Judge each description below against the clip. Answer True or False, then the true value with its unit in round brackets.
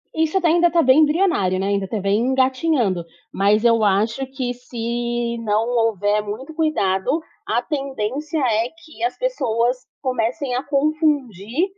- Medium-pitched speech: False (245 Hz)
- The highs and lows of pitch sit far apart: True (5.9 semitones)